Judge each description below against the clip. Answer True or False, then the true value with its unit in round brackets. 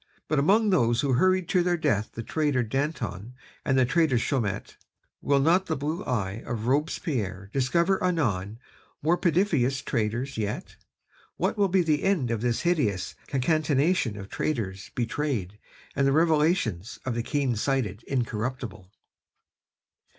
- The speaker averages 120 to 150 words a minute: True (145 wpm)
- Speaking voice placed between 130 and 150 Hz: True (135 Hz)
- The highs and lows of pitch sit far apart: True (6.0 semitones)